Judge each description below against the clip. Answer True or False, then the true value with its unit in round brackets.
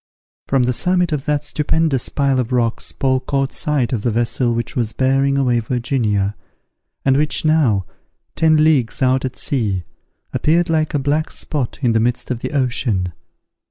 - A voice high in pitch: False (130 Hz)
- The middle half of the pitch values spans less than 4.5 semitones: True (3.9 semitones)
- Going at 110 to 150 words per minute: False (170 wpm)